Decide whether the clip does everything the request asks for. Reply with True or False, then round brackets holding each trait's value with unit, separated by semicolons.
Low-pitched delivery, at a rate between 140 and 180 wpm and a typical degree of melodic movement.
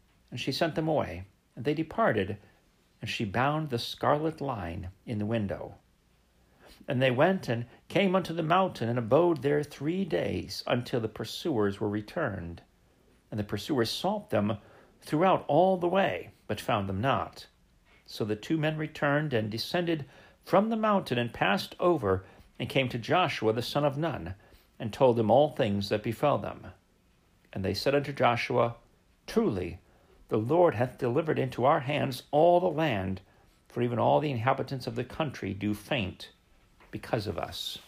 False (120 Hz; 170 wpm; 6.5 semitones)